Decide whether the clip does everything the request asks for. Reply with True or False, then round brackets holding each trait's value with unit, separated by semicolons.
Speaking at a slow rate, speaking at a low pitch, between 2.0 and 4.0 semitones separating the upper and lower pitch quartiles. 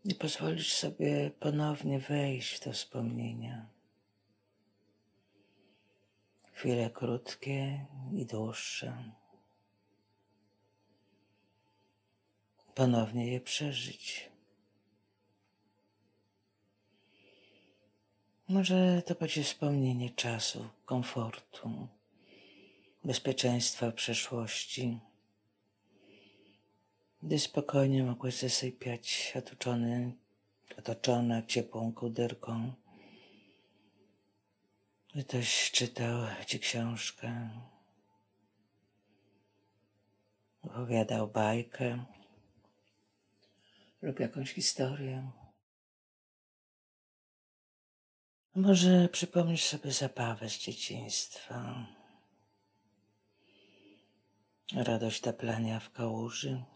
True (55 wpm; 105 Hz; 3.6 semitones)